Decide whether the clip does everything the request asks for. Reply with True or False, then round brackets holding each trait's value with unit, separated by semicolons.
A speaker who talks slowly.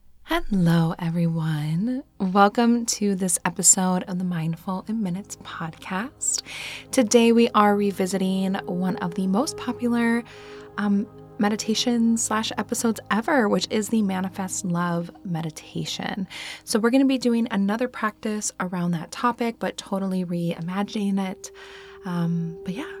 True (130 wpm)